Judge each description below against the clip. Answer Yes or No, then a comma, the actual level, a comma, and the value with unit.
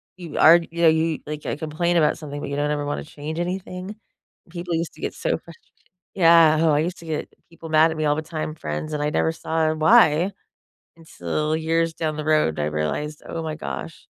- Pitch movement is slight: Yes, narrow, 1.7 semitones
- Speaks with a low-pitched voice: No, medium, 160 Hz